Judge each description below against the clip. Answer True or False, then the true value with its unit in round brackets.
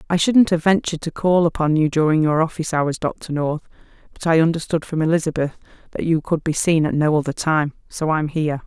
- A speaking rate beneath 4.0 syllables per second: False (5.9 syllables/s)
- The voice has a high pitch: False (160 Hz)